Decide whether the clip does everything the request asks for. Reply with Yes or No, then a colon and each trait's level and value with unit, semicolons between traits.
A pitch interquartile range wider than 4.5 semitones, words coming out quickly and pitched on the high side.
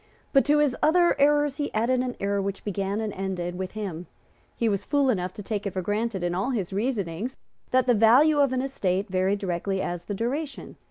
Yes: wide, 5.4 semitones; fast, 215 wpm; high, 210 Hz